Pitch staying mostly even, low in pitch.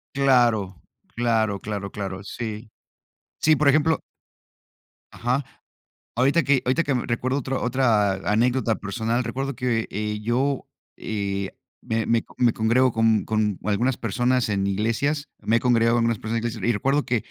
No: average, 3.2 semitones; low, 115 Hz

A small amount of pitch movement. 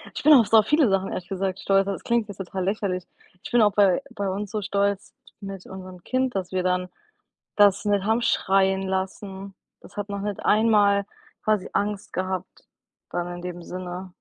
Yes: narrow, 1.7 semitones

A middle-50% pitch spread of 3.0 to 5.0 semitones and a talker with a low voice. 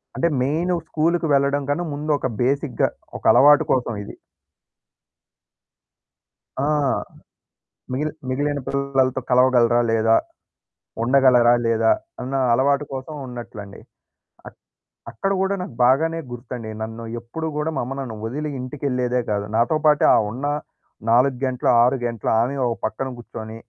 Yes: average, 3.3 semitones; low, 130 Hz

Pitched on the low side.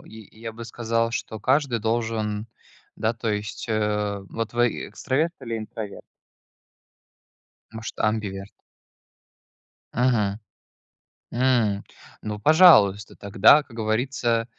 Yes: low, 110 Hz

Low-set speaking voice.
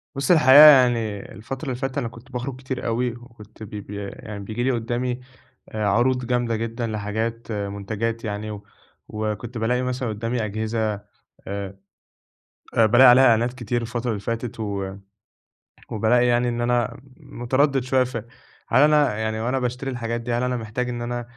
Yes: low, 120 Hz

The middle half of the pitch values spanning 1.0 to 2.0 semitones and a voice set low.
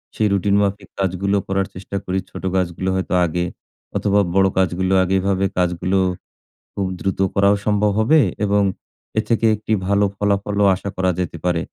Yes: narrow, 1.6 semitones; very low, 95 Hz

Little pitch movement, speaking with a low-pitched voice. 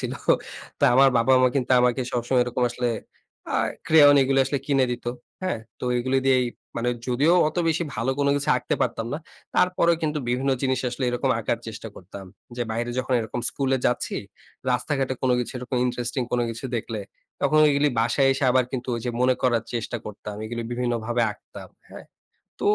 Yes: narrow, 2.3 semitones; low, 125 Hz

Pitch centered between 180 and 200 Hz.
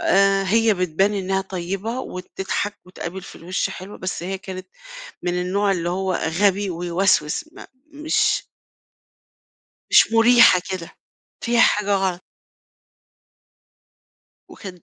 Yes: high, 190 Hz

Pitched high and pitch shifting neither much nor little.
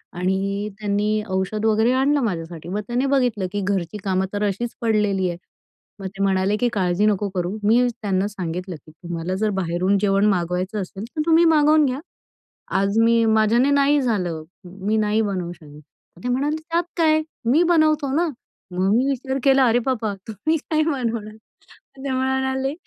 No: high, 210 Hz; wide, 5.7 semitones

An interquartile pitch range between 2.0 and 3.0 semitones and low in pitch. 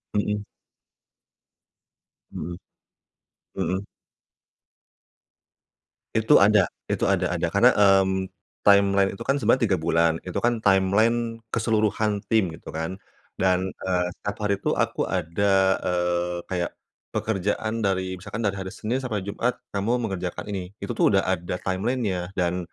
Yes: narrow, 2.6 semitones; very low, 95 Hz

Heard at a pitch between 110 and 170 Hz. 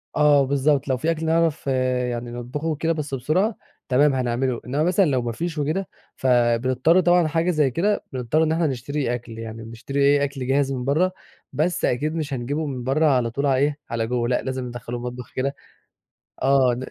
Yes: low, 135 Hz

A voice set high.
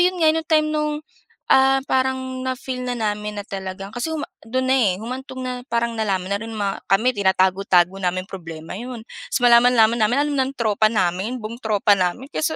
Yes: high, 230 Hz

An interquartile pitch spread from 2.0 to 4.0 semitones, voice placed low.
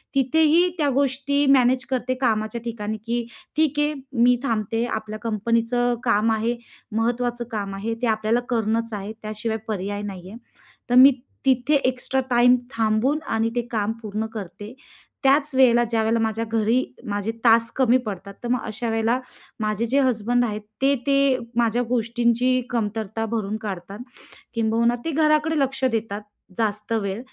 No: average, 2.7 semitones; high, 230 Hz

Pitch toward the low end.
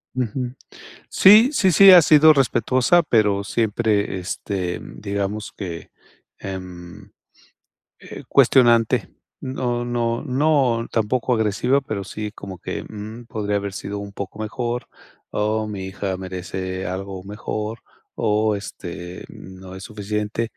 Yes: low, 105 Hz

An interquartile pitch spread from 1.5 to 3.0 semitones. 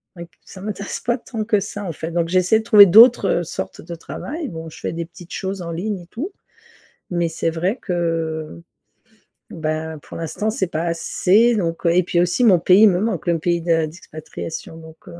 No: average, 3.7 semitones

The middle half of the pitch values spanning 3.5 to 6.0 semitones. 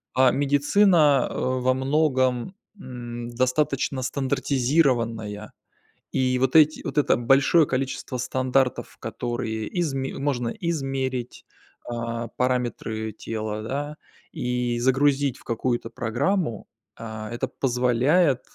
No: average, 2.7 semitones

